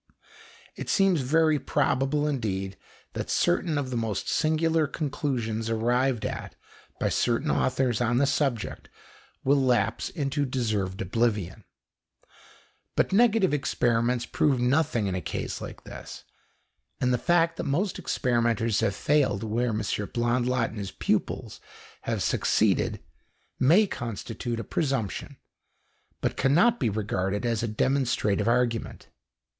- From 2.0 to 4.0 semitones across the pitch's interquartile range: No, average, 4.4 semitones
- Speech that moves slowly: Yes, slow, 130 wpm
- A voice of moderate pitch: No, low, 125 Hz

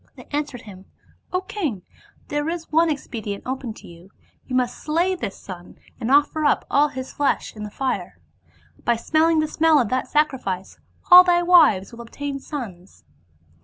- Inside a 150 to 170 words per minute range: No, average, 185 wpm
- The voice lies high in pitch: Yes, very high, 280 Hz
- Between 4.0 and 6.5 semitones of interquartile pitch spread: Yes, wide, 5.6 semitones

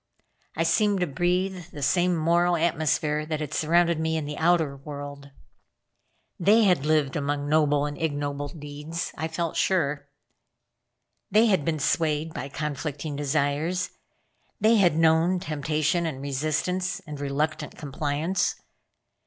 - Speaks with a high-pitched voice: No, medium, 155 Hz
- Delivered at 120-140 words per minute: Yes, slow, 135 wpm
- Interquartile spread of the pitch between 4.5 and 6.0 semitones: No, average, 3.0 semitones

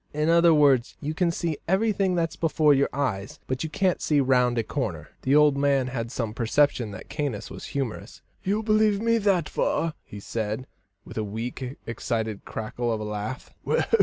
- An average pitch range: No, wide, 6.2 semitones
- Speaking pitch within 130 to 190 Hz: Yes, medium, 140 Hz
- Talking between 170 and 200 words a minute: Yes, average, 185 wpm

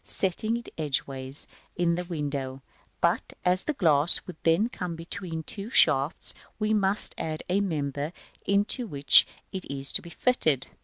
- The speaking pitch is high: No, medium, 170 Hz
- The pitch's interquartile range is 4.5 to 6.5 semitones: Yes, wide, 5.6 semitones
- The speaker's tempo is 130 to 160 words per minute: No, average, 185 wpm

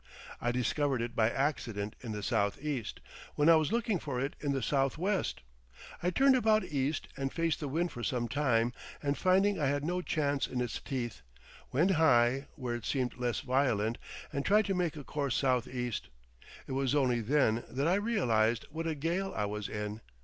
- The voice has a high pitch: No, low, 135 Hz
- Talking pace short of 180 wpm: No, average, 190 wpm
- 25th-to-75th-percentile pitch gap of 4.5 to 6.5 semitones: Yes, average, 5.1 semitones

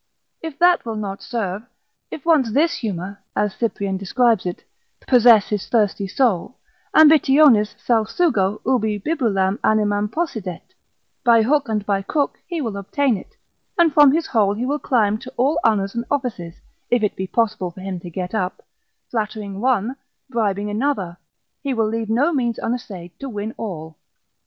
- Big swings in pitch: No, average, 4.7 semitones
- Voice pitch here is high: Yes, high, 220 Hz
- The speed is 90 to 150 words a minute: No, average, 160 wpm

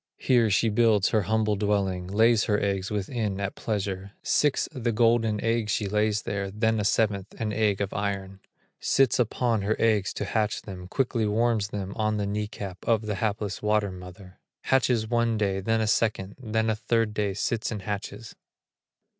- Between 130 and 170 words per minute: No, average, 180 wpm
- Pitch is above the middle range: No, low, 105 Hz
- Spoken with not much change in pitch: Yes, narrow, 2.1 semitones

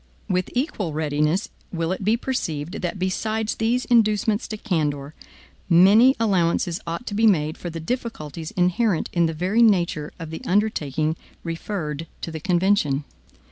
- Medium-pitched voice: Yes, medium, 180 Hz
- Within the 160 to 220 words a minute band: No, average, 150 wpm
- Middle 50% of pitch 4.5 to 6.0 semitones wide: Yes, average, 5.1 semitones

